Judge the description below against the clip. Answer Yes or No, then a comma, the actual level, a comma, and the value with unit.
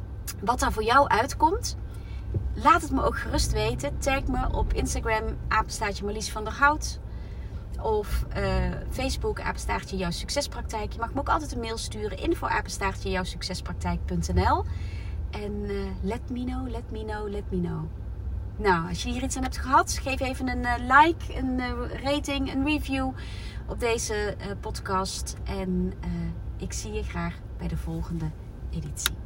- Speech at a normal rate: Yes, average, 165 wpm